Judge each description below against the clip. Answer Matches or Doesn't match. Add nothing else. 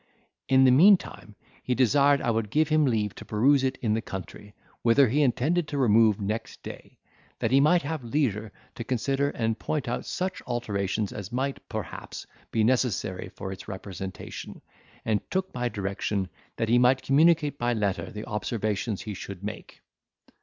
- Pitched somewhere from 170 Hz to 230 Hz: Doesn't match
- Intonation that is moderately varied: Matches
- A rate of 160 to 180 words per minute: Matches